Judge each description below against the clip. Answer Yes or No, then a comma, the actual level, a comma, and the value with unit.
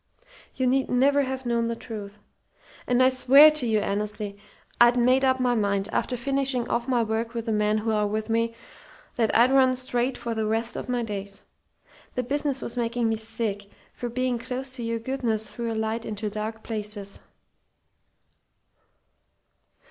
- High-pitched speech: Yes, high, 230 Hz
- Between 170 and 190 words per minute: Yes, average, 175 wpm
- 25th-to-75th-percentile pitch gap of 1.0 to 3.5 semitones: Yes, average, 2.7 semitones